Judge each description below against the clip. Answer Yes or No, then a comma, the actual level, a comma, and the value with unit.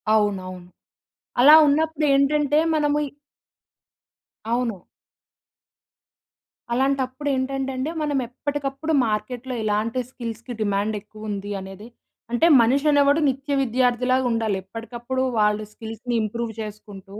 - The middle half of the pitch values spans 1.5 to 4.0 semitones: No, average, 4.4 semitones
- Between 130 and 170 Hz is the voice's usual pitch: No, high, 245 Hz